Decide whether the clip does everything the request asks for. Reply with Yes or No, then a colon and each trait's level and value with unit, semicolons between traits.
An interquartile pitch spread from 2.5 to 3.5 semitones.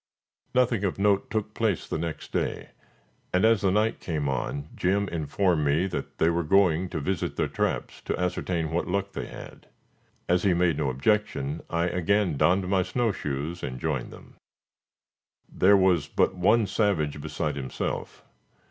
No: average, 4.3 semitones